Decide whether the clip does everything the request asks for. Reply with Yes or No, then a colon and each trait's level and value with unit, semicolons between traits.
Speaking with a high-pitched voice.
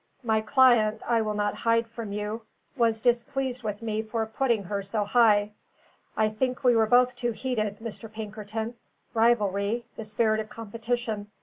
Yes: high, 225 Hz